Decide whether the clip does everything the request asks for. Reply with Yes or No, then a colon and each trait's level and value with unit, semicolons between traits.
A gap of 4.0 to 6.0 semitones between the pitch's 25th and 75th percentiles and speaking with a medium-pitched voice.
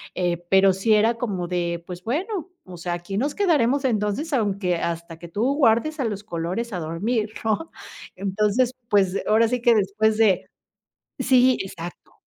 No: average, 5.0 semitones; high, 210 Hz